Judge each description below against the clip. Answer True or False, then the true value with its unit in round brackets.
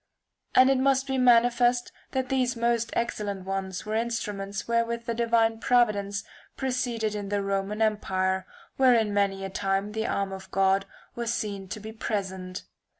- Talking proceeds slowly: False (155 wpm)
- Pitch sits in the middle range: False (220 Hz)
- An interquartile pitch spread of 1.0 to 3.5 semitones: True (3.2 semitones)